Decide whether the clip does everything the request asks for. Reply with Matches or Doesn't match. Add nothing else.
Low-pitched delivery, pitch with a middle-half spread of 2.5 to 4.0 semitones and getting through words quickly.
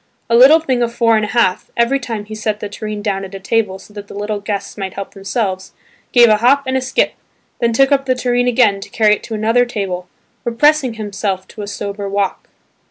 Doesn't match